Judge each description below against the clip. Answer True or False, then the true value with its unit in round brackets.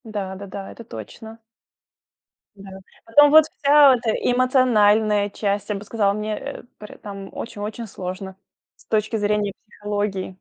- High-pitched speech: True (210 Hz)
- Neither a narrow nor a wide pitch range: False (2.2 semitones)